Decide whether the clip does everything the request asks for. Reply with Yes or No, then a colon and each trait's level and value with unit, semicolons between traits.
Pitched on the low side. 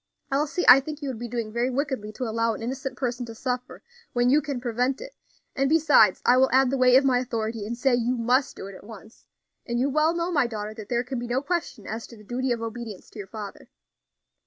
No: high, 245 Hz